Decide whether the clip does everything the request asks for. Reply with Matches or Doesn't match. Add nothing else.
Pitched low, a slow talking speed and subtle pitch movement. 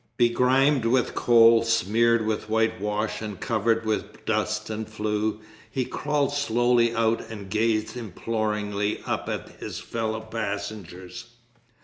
Matches